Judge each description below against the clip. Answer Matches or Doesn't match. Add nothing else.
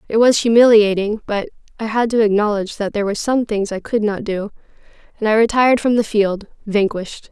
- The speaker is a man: Doesn't match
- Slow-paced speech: Doesn't match